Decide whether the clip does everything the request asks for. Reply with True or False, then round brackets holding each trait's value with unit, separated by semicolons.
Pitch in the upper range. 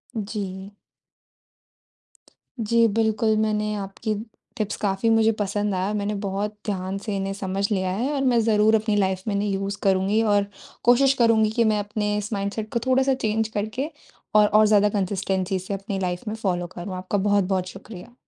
True (205 Hz)